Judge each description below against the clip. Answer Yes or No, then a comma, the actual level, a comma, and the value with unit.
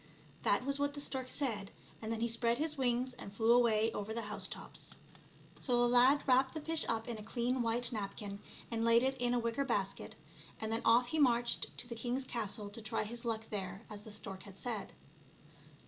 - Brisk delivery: Yes, fast, 220 wpm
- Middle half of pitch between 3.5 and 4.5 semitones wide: No, narrow, 2.4 semitones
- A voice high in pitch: Yes, high, 235 Hz